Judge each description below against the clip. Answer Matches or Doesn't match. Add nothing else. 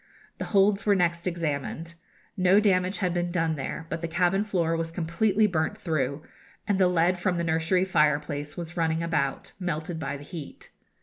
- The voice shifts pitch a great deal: Doesn't match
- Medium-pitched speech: Matches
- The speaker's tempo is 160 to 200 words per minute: Matches